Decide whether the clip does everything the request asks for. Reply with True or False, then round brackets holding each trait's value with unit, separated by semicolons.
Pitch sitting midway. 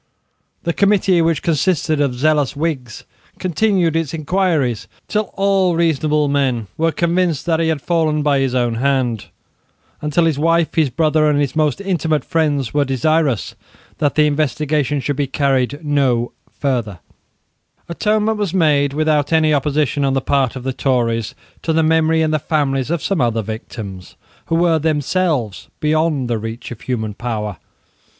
True (150 Hz)